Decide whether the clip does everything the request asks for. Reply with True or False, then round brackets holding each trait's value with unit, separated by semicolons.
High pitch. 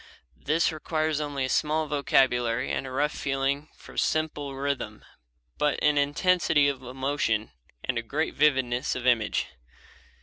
False (140 Hz)